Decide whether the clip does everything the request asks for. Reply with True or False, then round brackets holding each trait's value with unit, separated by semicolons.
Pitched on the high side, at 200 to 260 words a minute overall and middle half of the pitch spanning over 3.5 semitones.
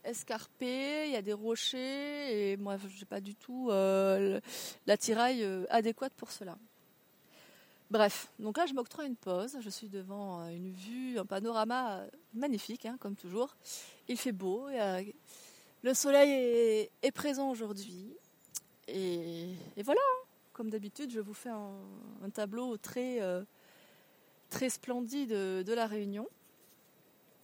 False (225 Hz; 150 wpm; 4.1 semitones)